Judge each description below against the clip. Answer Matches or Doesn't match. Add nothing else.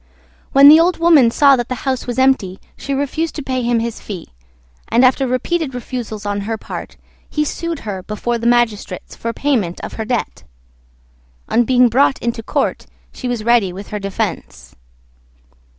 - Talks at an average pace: Matches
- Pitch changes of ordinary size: Matches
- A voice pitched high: Matches